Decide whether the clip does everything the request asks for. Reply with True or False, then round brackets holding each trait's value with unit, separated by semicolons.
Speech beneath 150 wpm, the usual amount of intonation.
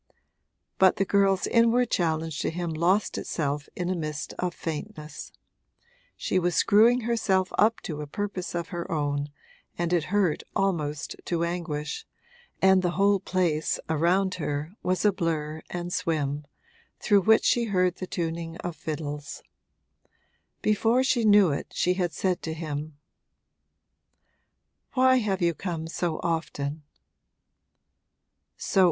True (135 wpm; 3.7 semitones)